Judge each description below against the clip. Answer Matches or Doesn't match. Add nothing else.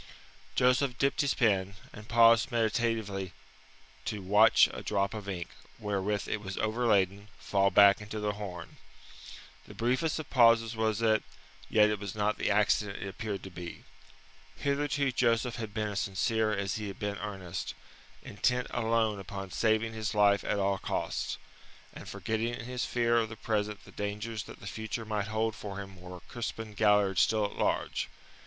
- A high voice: Doesn't match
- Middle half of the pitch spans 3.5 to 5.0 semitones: Doesn't match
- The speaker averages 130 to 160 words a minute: Doesn't match